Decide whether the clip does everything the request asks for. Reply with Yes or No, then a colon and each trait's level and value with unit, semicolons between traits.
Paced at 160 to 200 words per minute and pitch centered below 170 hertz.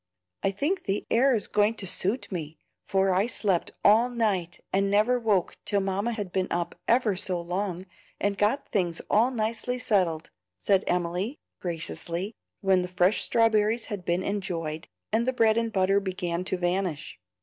No: average, 170 wpm; high, 195 Hz